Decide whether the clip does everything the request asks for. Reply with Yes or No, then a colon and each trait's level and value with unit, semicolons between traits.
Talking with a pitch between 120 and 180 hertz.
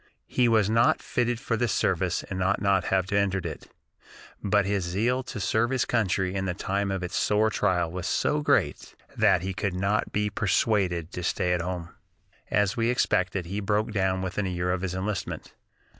No: very low, 95 Hz